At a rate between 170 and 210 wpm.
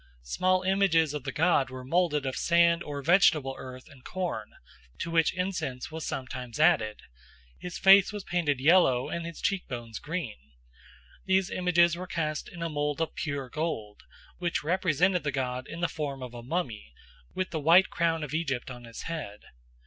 Yes: average, 180 wpm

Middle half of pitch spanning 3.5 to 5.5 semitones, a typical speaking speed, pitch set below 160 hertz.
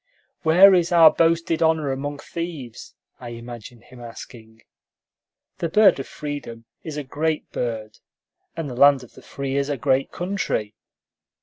Yes: average, 5.1 semitones; average, 150 wpm; medium, 140 Hz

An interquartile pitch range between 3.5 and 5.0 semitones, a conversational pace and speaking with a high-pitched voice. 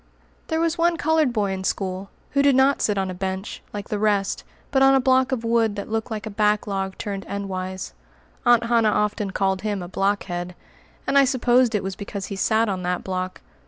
No: average, 3.9 semitones; fast, 210 wpm; high, 210 Hz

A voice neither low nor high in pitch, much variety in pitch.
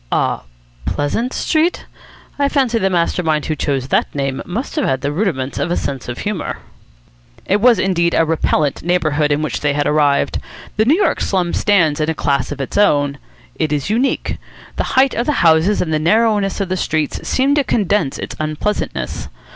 Yes: medium, 170 Hz; wide, 6.2 semitones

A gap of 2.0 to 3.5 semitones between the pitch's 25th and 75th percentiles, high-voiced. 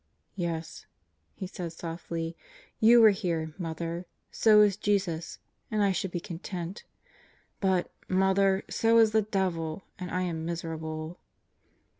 No: average, 3.1 semitones; medium, 180 Hz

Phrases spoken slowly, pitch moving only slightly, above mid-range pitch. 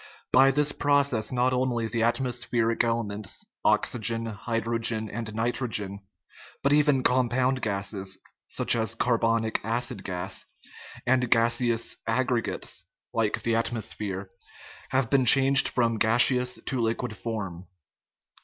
No: slow, 115 wpm; narrow, 2.2 semitones; low, 115 Hz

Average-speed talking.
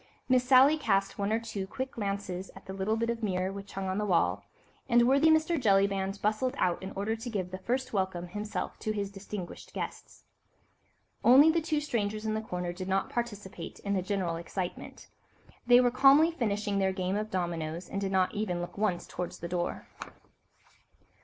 Yes: average, 190 wpm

